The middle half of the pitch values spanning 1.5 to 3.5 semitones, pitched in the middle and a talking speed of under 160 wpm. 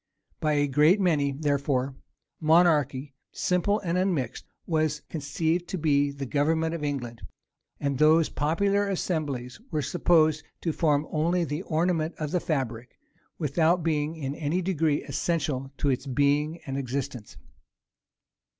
Yes: average, 2.9 semitones; medium, 155 Hz; slow, 135 wpm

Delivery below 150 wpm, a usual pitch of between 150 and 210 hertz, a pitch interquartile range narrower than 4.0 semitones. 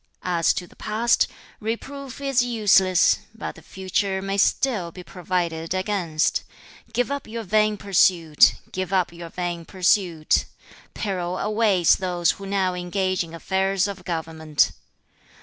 Yes: slow, 135 wpm; medium, 185 Hz; average, 3.2 semitones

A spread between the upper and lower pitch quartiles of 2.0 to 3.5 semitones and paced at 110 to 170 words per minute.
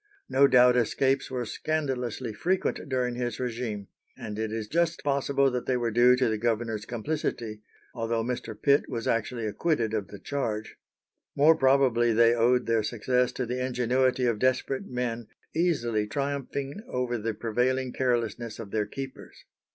Yes: narrow, 2.5 semitones; average, 160 wpm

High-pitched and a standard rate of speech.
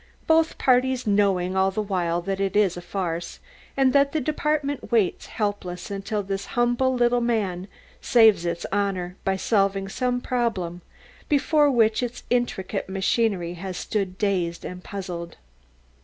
Yes: high, 200 Hz; average, 145 wpm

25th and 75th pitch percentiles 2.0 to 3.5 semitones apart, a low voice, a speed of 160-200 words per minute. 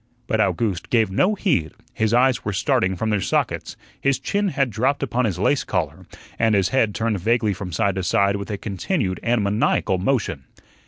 No: average, 4.2 semitones; low, 110 Hz; average, 195 wpm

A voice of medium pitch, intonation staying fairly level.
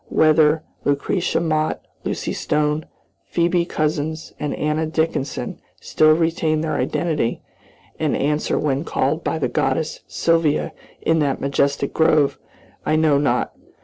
Yes: medium, 155 Hz; narrow, 1.8 semitones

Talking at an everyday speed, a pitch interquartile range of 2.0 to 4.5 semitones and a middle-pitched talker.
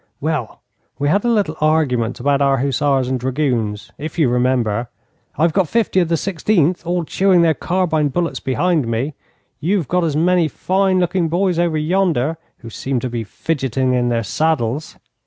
No: average, 175 wpm; average, 5.3 semitones; medium, 155 Hz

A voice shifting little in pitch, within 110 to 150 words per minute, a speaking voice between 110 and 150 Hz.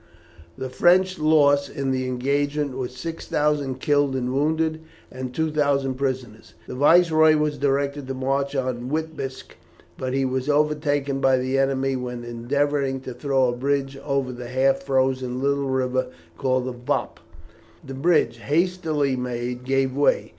Yes: narrow, 2.0 semitones; average, 145 wpm; low, 135 Hz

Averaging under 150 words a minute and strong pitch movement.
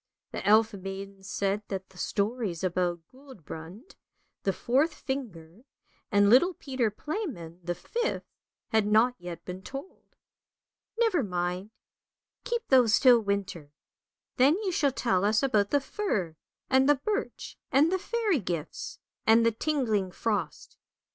Yes: average, 140 wpm; wide, 6.6 semitones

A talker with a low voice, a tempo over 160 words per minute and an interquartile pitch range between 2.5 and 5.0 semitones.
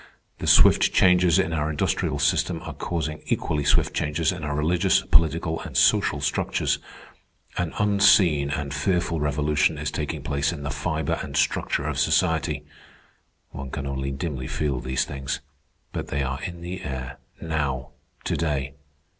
No: very low, 75 Hz; average, 155 wpm; average, 2.8 semitones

